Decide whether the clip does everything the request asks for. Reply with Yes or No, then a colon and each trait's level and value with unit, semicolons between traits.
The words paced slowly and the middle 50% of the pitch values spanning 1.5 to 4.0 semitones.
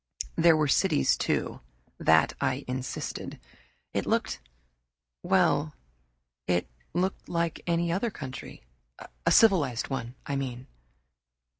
No: slow, 110 wpm; average, 5.0 semitones